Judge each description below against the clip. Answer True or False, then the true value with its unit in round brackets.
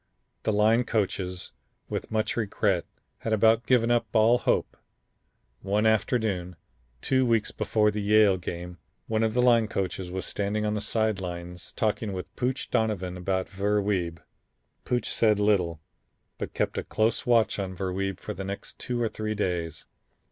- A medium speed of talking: True (165 wpm)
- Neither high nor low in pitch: False (105 Hz)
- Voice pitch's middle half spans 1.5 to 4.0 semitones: True (3.0 semitones)